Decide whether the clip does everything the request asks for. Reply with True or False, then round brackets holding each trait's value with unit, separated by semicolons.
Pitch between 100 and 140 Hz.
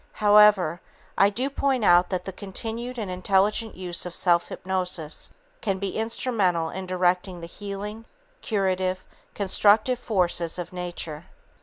False (190 Hz)